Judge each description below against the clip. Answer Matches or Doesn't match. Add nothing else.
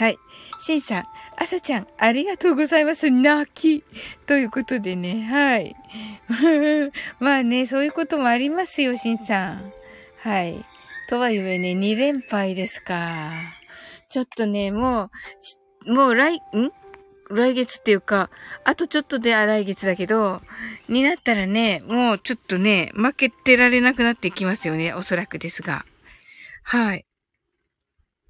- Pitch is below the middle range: Doesn't match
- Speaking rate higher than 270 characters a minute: Matches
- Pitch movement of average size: Doesn't match